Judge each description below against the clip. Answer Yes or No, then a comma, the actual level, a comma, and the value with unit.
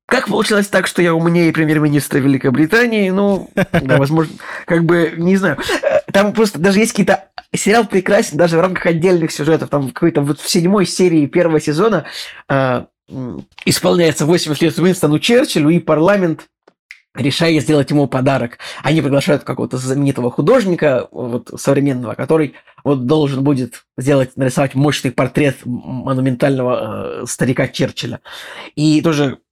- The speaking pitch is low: No, medium, 155 Hz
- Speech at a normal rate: Yes, average, 135 wpm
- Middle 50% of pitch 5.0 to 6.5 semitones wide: No, average, 4.5 semitones